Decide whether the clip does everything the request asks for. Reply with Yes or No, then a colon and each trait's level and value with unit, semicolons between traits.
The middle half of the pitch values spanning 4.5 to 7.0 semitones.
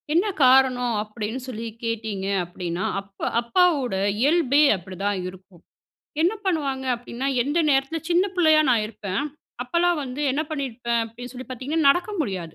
Yes: wide, 5.5 semitones